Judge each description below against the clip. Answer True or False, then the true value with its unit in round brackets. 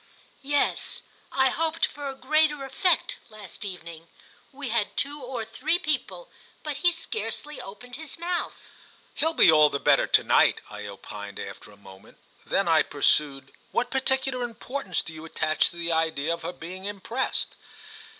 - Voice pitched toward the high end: True (240 Hz)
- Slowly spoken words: False (160 wpm)